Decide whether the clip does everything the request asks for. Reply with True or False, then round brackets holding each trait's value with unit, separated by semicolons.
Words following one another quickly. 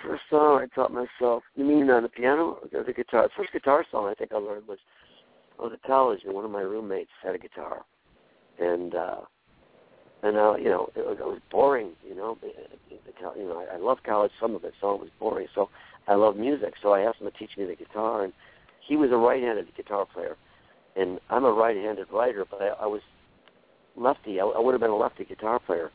True (225 wpm)